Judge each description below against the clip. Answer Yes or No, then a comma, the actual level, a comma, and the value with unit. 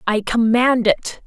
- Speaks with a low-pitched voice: No, high, 230 Hz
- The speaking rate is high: No, average, 140 wpm